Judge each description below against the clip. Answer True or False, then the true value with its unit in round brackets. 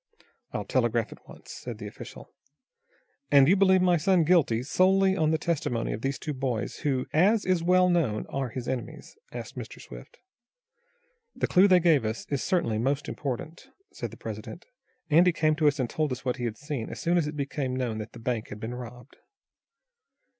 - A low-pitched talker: False (145 Hz)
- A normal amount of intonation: False (5.8 semitones)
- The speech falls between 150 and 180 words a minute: False (195 wpm)